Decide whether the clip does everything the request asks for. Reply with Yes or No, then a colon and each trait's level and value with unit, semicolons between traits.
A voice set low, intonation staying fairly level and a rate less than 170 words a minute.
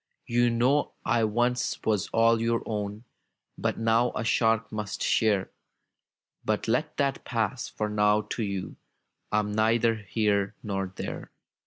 Yes: low, 110 Hz; narrow, 2.0 semitones; average, 145 wpm